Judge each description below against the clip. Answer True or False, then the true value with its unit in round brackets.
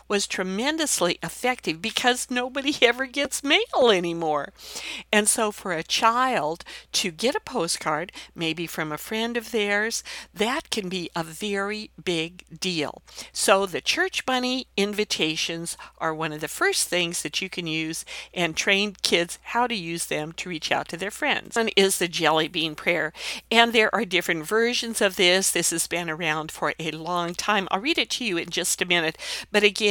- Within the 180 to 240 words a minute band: True (185 wpm)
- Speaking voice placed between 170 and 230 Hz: True (190 Hz)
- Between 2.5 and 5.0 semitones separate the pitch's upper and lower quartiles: False (5.5 semitones)